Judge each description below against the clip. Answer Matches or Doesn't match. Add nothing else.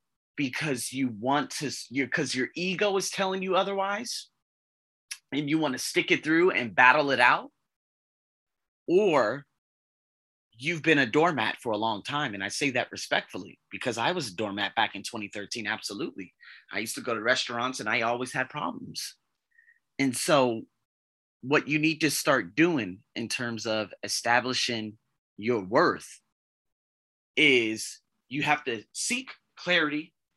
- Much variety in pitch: Matches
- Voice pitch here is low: Matches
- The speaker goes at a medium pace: Matches